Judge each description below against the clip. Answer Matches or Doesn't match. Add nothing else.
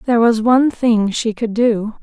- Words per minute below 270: Matches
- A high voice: Matches